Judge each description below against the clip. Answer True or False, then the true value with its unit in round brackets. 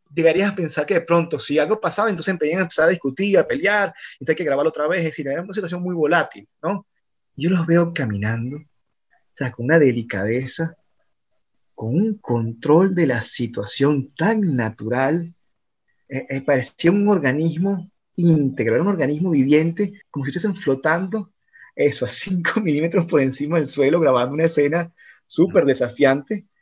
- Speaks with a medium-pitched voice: True (160 Hz)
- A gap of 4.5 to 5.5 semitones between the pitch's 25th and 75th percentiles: True (5.1 semitones)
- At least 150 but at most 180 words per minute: True (160 wpm)